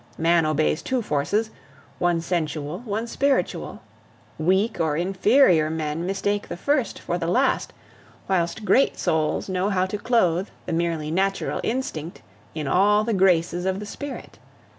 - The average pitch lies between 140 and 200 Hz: Yes, medium, 185 Hz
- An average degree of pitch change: Yes, average, 4.2 semitones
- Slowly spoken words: No, average, 145 wpm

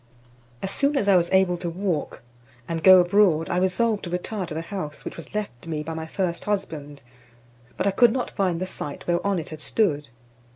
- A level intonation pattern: No, average, 3.6 semitones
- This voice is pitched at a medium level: Yes, medium, 180 Hz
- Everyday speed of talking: No, fast, 210 wpm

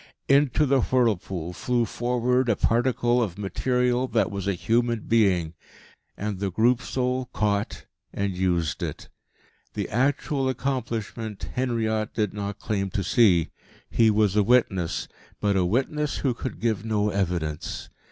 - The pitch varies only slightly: No, average, 3.9 semitones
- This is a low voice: Yes, low, 110 Hz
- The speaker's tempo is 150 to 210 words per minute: No, average, 140 wpm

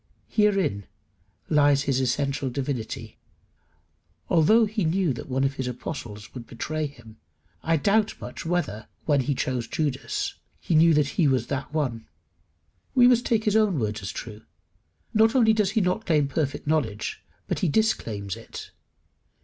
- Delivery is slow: No, average, 155 wpm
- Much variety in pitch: Yes, wide, 6.9 semitones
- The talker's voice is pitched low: No, medium, 145 Hz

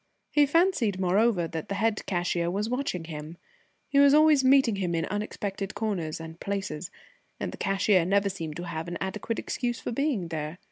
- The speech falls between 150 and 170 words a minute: No, average, 185 wpm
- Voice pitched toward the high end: Yes, high, 195 Hz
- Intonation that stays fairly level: No, average, 5.1 semitones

